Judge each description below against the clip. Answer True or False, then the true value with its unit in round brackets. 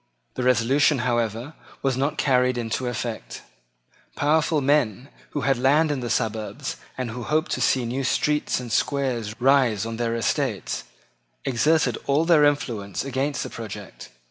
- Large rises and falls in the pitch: False (3.7 semitones)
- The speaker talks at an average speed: True (150 wpm)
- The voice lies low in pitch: True (130 Hz)